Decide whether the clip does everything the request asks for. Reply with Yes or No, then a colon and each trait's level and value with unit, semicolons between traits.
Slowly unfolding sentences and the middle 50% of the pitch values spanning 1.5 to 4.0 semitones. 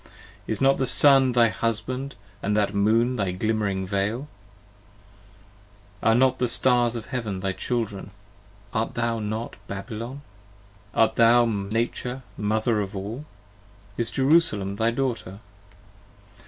Yes: slow, 125 wpm; average, 3.2 semitones